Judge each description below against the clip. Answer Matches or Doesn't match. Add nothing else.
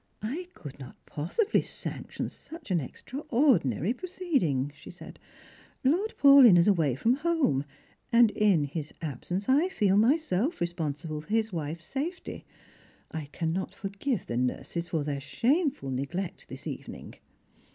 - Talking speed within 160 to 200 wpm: Doesn't match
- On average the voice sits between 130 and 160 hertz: Doesn't match